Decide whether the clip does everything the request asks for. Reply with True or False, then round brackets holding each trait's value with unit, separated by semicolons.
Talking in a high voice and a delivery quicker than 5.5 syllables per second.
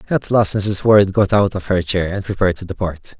False (100 Hz; 5.7 syllables/s)